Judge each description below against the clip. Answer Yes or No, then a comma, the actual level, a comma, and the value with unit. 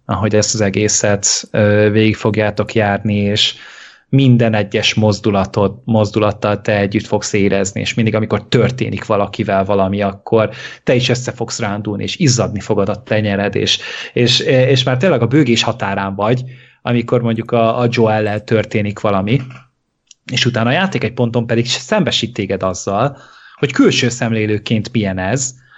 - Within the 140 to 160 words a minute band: Yes, average, 150 wpm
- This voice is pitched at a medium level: No, low, 110 Hz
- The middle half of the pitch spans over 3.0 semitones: No, average, 2.7 semitones